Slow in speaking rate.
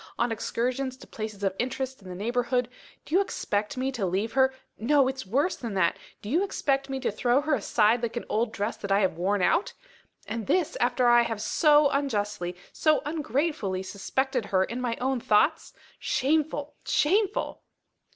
No: average, 180 wpm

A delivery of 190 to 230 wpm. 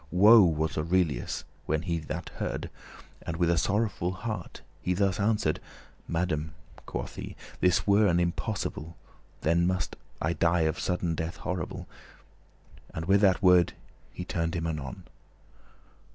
No: average, 145 wpm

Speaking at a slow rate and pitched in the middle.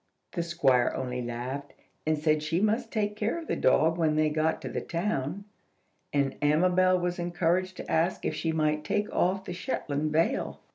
No: average, 185 wpm; medium, 165 Hz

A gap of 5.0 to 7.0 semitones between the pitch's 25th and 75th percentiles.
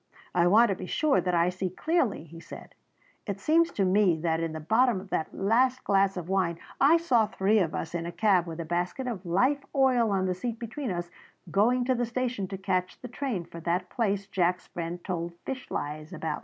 Yes: wide, 5.6 semitones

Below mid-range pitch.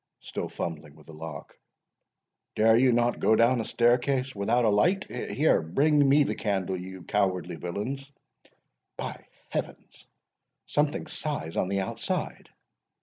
Yes: low, 110 Hz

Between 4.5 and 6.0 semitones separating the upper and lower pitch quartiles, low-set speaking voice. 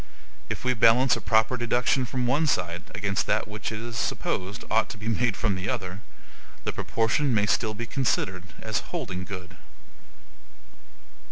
No: average, 3.8 semitones; low, 110 Hz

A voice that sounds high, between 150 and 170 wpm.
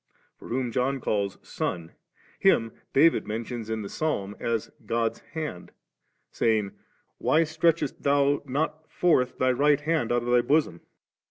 No: low, 125 Hz; average, 155 wpm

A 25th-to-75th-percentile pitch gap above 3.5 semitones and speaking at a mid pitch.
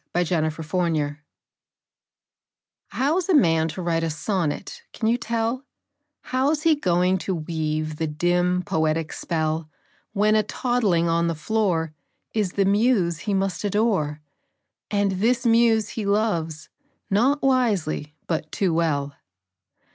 Yes: wide, 5.5 semitones; medium, 180 Hz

